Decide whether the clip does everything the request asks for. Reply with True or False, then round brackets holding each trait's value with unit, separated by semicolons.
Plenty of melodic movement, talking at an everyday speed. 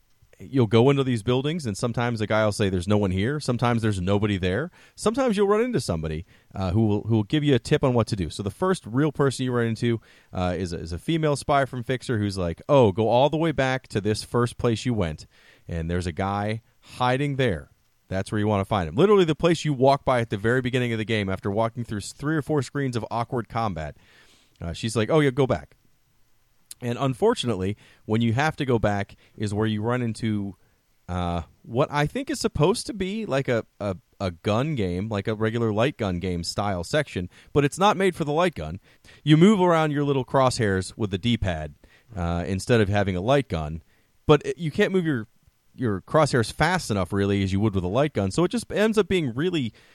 False (6.1 semitones; 235 wpm)